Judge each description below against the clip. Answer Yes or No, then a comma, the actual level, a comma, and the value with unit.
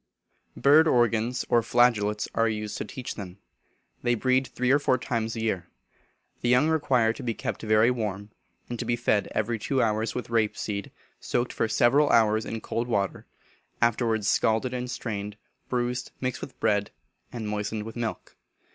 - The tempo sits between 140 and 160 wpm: No, average, 175 wpm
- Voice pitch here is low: Yes, low, 115 Hz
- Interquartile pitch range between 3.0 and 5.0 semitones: No, narrow, 2.5 semitones